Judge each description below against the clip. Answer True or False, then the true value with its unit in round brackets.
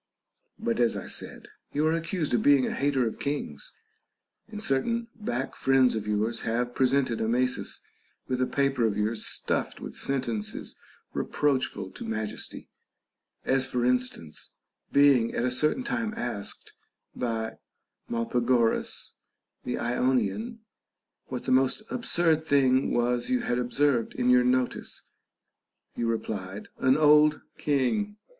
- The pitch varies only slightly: False (3.5 semitones)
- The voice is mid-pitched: False (130 Hz)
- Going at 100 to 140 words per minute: True (135 wpm)